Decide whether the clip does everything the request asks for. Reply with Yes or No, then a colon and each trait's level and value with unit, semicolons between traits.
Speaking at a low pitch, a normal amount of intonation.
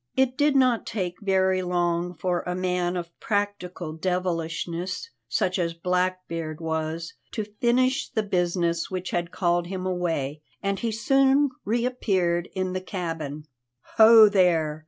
No: medium, 180 Hz; average, 3.1 semitones